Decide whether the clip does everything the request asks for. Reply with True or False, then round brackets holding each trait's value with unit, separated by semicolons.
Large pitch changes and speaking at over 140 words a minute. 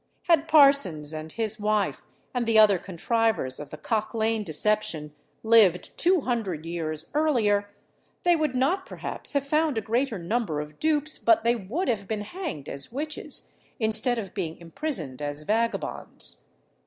True (7.6 semitones; 155 wpm)